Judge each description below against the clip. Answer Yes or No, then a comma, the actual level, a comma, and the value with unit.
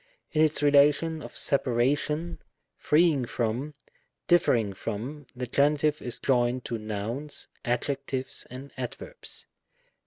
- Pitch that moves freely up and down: No, average, 3.7 semitones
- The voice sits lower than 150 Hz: Yes, medium, 140 Hz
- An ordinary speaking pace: No, slow, 115 wpm